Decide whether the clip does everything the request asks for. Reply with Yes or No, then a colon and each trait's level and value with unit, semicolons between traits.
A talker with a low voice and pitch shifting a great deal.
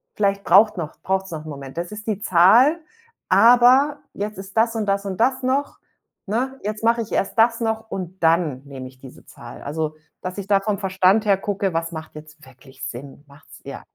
No: high, 195 Hz; wide, 5.8 semitones